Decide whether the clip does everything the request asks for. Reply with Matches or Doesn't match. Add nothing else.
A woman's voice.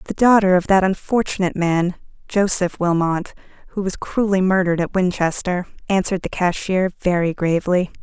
Matches